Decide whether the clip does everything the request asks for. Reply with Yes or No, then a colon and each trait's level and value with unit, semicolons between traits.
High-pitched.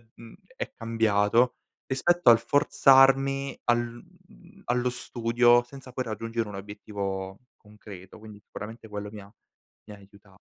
No: low, 115 Hz